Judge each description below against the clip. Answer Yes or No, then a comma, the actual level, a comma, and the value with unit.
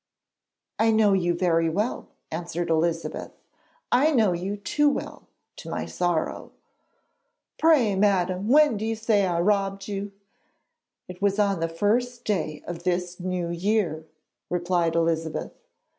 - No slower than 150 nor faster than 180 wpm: No, slow, 135 wpm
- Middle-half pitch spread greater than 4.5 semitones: No, average, 3.5 semitones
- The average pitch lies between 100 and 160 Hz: No, medium, 185 Hz